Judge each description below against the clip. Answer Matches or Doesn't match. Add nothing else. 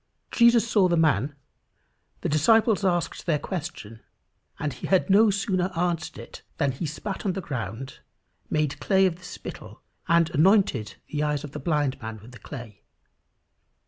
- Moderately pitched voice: Matches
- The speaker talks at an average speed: Matches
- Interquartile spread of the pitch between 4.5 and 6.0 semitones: Matches